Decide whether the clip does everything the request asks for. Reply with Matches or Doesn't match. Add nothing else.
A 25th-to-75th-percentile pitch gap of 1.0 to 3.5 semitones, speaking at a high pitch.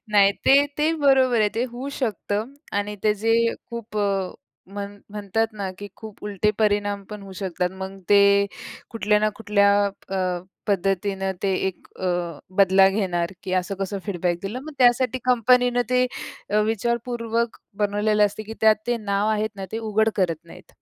Matches